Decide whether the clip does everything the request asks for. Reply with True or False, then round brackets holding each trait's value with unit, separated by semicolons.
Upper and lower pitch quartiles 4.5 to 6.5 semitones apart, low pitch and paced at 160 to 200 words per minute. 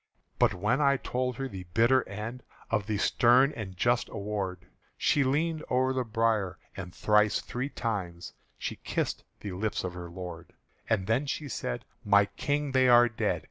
True (5.1 semitones; 115 Hz; 175 wpm)